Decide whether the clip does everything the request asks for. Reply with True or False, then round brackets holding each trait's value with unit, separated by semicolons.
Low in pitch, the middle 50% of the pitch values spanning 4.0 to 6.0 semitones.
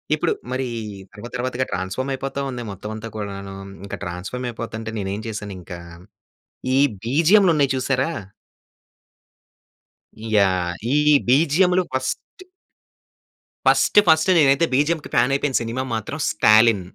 True (125 Hz; 5.1 semitones)